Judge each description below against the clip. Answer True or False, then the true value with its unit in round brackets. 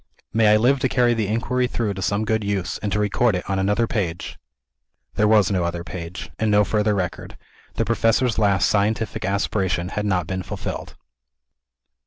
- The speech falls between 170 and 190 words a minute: True (185 wpm)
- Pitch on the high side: False (105 Hz)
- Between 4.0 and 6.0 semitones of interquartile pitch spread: False (2.8 semitones)